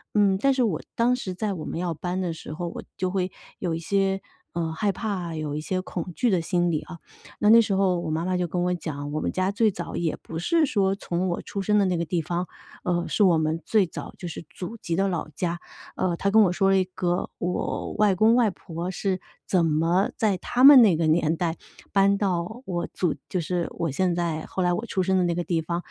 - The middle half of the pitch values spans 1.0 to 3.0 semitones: Yes, narrow, 2.6 semitones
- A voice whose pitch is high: No, medium, 180 Hz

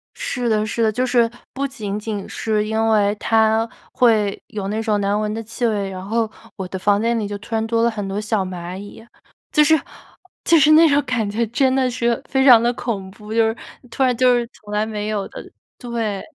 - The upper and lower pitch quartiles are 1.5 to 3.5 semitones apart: Yes, narrow, 2.5 semitones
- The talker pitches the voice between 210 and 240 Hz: Yes, high, 220 Hz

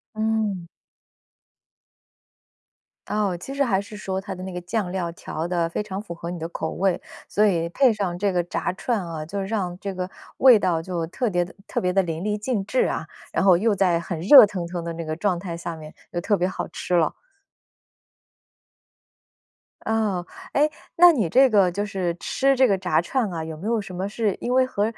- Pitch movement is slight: No, average, 3.5 semitones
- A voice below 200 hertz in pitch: Yes, high, 190 Hz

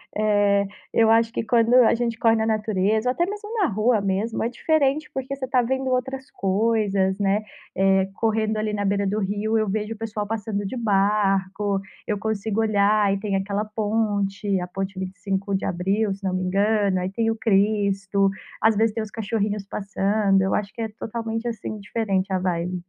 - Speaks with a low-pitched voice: No, high, 210 Hz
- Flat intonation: Yes, narrow, 2.3 semitones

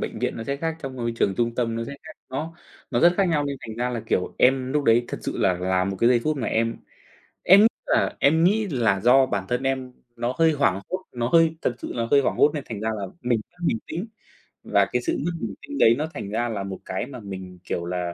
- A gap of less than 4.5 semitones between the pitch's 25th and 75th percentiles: No, average, 5.1 semitones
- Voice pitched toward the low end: Yes, low, 125 Hz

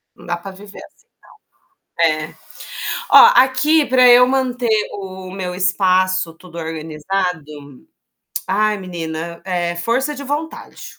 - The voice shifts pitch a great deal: Yes, wide, 6.4 semitones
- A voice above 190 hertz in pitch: No, medium, 185 Hz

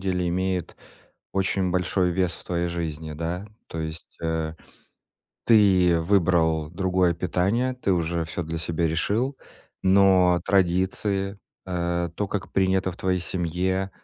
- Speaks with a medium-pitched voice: No, very low, 90 Hz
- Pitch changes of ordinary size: No, narrow, 2.1 semitones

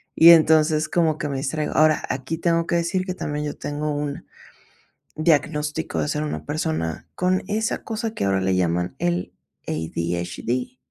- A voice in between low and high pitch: Yes, medium, 150 Hz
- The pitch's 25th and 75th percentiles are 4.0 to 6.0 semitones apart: Yes, average, 4.7 semitones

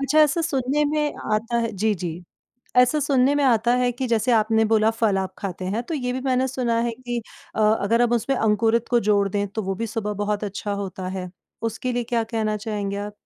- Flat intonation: No, average, 3.2 semitones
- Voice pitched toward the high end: Yes, high, 225 Hz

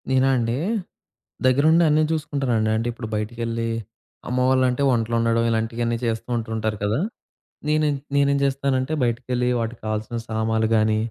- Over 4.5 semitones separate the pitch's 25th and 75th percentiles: No, average, 2.8 semitones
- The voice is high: No, low, 120 Hz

